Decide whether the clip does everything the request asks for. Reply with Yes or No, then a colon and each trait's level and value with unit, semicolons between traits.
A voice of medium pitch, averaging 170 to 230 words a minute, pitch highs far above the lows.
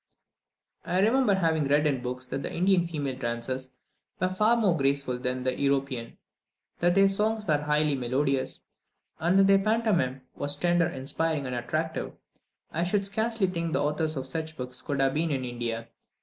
Yes: medium, 150 Hz; average, 175 wpm; wide, 5.7 semitones